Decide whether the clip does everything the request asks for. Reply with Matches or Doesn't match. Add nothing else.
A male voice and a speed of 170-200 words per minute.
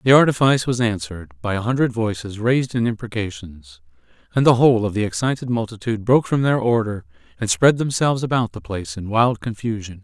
Matches